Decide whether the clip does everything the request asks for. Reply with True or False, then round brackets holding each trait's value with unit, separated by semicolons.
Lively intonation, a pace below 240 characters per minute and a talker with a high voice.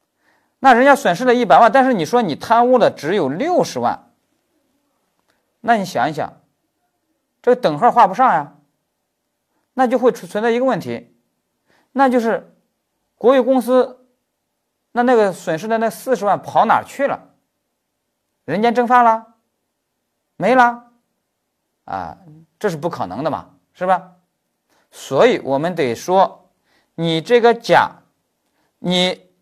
True (5.7 semitones; 190 characters per minute; 235 Hz)